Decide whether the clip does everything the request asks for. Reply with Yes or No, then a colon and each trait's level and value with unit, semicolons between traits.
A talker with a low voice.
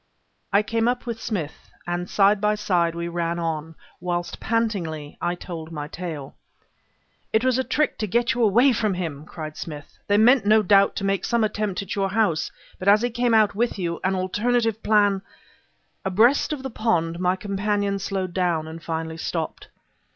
No: high, 195 Hz